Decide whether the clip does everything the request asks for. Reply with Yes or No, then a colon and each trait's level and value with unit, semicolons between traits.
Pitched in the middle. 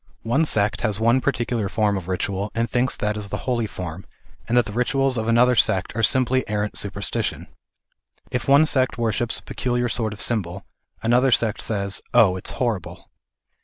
No: low, 115 Hz